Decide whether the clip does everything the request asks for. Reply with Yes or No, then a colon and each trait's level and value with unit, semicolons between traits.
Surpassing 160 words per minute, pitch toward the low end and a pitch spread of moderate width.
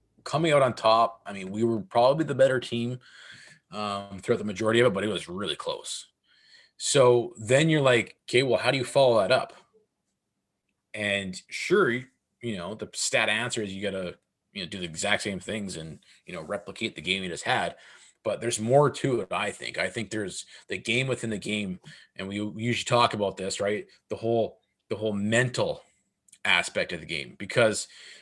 Yes: average, 200 wpm; low, 115 Hz; average, 3.5 semitones